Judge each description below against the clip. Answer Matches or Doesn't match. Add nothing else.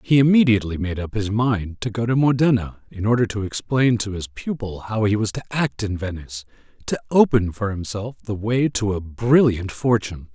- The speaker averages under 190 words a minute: Doesn't match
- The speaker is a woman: Doesn't match